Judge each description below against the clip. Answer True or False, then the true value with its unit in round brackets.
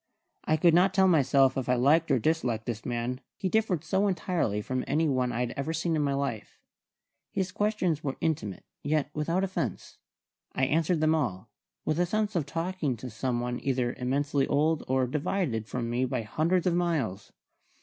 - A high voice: False (145 Hz)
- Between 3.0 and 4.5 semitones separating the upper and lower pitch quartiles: False (5.1 semitones)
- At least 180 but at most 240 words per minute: True (190 wpm)